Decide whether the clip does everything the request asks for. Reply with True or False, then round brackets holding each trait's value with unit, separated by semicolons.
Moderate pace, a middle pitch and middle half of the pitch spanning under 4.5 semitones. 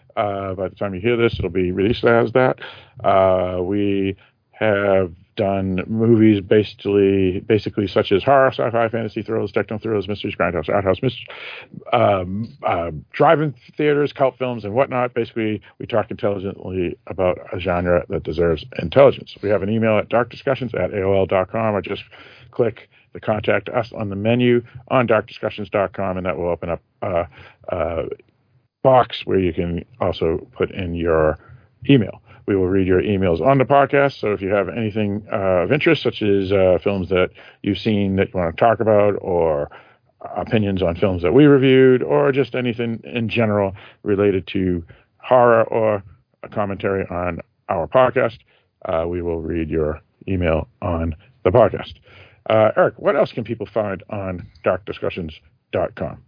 False (165 wpm; 105 Hz; 3.7 semitones)